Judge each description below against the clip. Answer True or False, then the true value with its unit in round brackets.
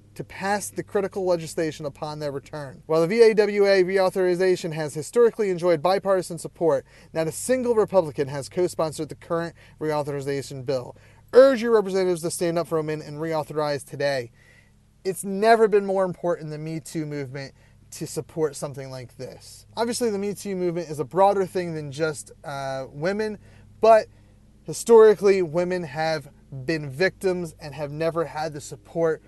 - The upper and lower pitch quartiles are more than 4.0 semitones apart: True (4.4 semitones)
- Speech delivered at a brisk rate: False (160 wpm)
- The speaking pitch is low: False (160 Hz)